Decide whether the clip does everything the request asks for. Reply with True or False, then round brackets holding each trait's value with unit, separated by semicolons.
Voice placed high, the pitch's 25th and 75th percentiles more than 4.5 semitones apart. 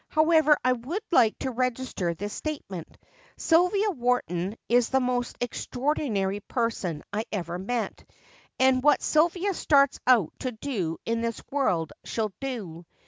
True (245 Hz; 5.5 semitones)